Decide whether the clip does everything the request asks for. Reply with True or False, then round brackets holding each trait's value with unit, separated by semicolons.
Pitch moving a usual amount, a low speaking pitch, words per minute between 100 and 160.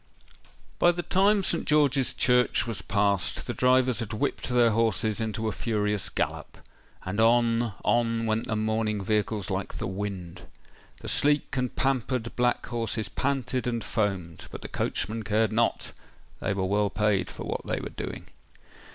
True (3.0 semitones; 115 Hz; 150 wpm)